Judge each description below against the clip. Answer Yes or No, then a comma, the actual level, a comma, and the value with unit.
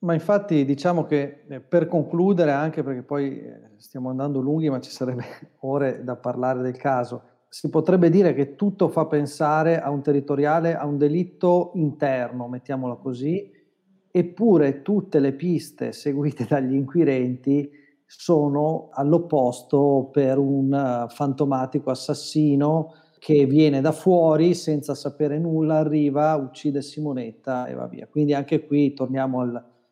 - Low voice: No, medium, 145 Hz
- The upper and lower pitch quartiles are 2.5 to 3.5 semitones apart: Yes, average, 2.9 semitones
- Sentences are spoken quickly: No, average, 135 wpm